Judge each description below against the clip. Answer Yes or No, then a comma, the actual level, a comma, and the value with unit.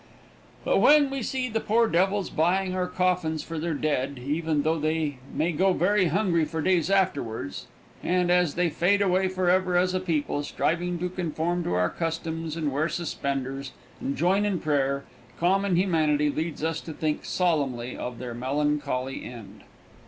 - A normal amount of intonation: Yes, average, 3.9 semitones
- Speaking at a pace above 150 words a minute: Yes, average, 165 wpm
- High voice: No, medium, 165 Hz